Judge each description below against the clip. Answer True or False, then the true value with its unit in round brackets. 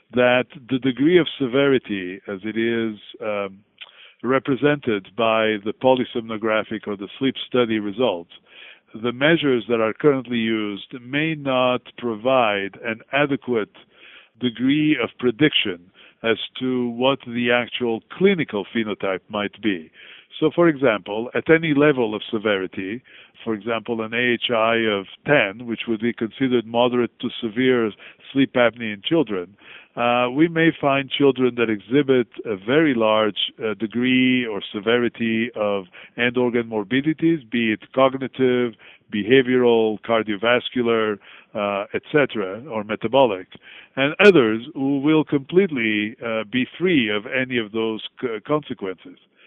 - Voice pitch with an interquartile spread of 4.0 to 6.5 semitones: False (3.3 semitones)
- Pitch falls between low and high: False (120 Hz)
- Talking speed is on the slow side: True (130 wpm)